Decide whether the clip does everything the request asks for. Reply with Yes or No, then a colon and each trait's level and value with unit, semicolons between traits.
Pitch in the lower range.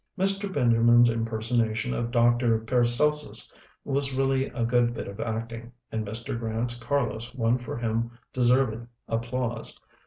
Yes: low, 120 Hz